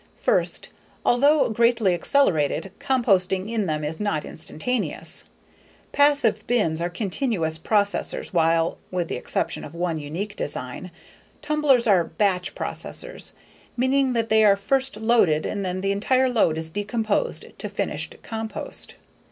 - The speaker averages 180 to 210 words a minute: No, slow, 135 wpm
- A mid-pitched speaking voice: No, high, 205 Hz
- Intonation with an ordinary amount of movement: No, wide, 5.9 semitones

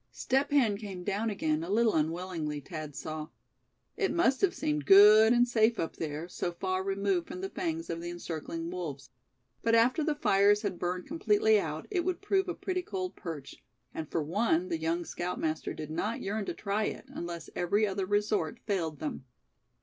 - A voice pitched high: Yes, high, 195 Hz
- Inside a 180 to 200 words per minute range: Yes, average, 190 wpm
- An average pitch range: No, wide, 5.7 semitones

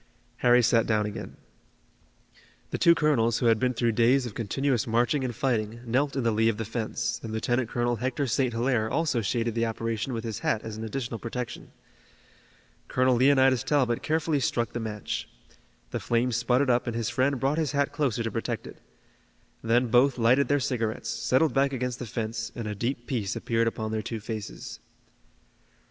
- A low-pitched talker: Yes, low, 120 Hz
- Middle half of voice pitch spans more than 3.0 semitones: No, narrow, 2.5 semitones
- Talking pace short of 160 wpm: No, average, 190 wpm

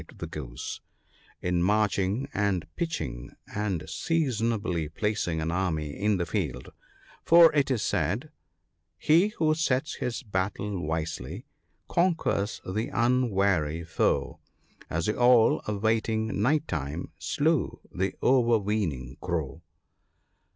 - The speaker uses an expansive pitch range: Yes, wide, 6.6 semitones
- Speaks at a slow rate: Yes, slow, 120 wpm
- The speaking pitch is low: Yes, low, 100 Hz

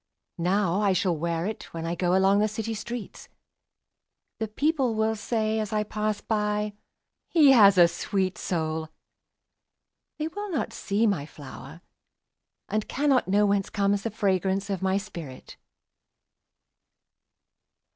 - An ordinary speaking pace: No, slow, 110 wpm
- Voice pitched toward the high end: Yes, high, 205 Hz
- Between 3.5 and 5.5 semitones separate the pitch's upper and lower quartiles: No, average, 2.8 semitones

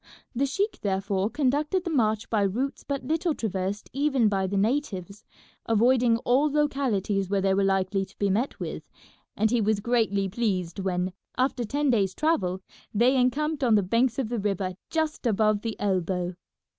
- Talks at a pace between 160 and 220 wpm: Yes, average, 170 wpm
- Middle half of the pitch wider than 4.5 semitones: Yes, wide, 5.4 semitones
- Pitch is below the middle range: No, high, 220 Hz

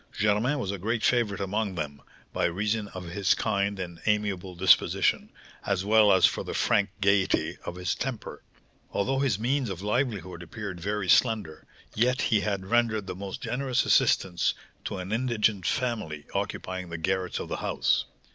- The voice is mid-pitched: No, low, 100 Hz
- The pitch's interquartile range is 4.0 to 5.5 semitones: No, average, 3.1 semitones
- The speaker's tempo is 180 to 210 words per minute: No, average, 165 wpm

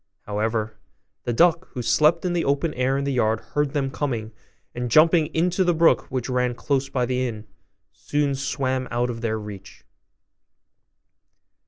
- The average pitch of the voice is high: No, low, 130 Hz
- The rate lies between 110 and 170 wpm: Yes, average, 165 wpm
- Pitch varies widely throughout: No, average, 4.0 semitones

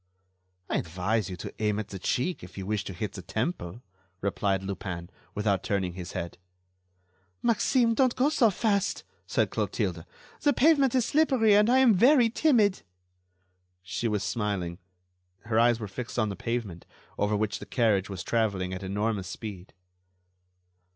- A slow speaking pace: No, average, 160 wpm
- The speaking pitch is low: Yes, low, 105 Hz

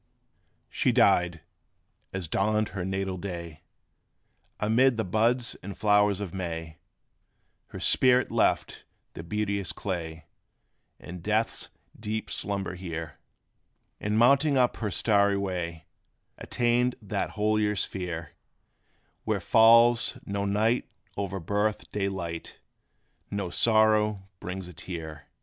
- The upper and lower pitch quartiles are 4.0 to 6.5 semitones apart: No, average, 3.4 semitones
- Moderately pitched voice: No, low, 100 Hz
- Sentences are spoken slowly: Yes, slow, 115 wpm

